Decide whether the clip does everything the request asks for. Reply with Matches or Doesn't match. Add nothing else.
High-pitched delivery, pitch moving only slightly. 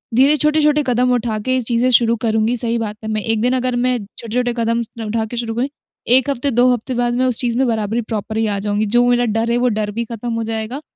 Matches